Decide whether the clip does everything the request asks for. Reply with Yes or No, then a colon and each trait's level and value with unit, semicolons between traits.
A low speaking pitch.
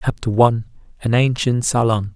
Yes: low, 115 Hz